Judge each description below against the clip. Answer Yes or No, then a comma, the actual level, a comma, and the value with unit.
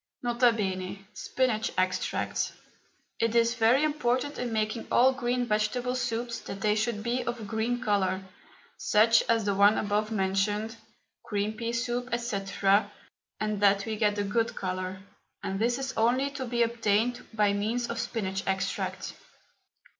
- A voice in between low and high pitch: No, high, 225 Hz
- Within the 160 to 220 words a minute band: No, average, 150 wpm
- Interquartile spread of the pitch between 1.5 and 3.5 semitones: Yes, average, 2.8 semitones